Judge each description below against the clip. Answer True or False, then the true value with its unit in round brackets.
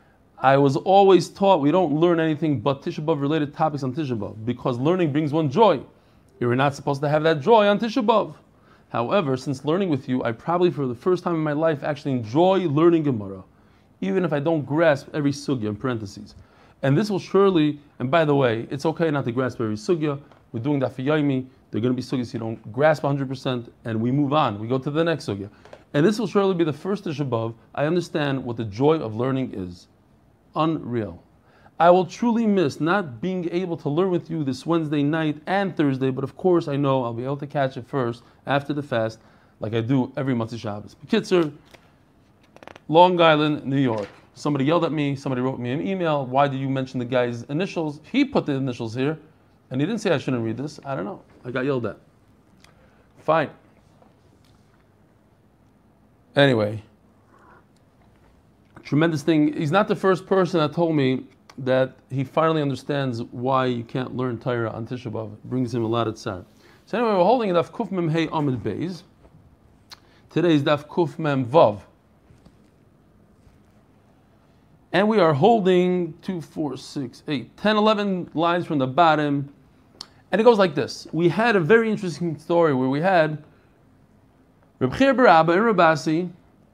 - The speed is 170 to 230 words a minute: True (190 wpm)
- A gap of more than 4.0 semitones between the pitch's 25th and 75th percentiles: True (5.1 semitones)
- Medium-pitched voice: True (145 Hz)